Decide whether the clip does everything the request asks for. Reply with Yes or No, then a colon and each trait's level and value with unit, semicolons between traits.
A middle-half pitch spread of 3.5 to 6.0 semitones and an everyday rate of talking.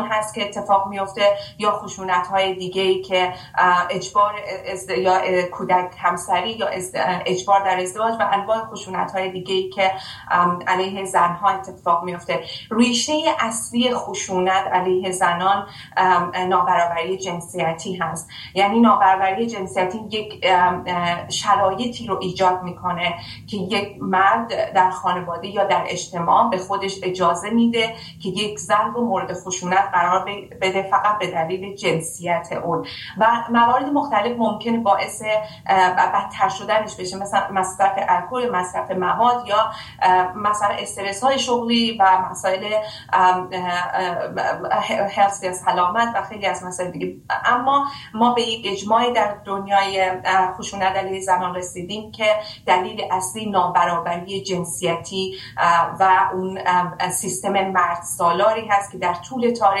No: narrow, 2.4 semitones; average, 125 wpm